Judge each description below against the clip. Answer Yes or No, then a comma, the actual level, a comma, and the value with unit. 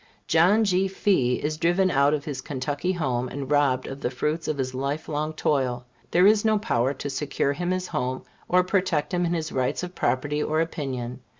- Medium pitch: Yes, medium, 150 Hz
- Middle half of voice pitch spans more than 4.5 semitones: Yes, average, 5.1 semitones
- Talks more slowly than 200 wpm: No, fast, 205 wpm